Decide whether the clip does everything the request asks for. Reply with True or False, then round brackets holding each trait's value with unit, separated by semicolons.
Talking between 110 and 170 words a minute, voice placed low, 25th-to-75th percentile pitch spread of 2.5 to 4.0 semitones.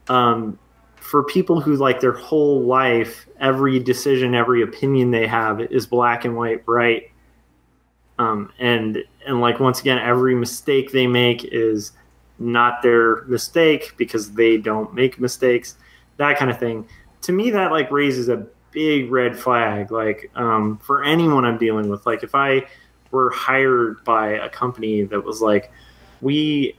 True (155 wpm; 120 Hz; 3.0 semitones)